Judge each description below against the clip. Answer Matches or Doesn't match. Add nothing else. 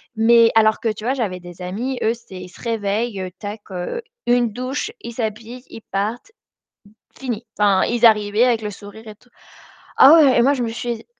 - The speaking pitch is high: Matches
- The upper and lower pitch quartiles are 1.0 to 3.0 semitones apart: Matches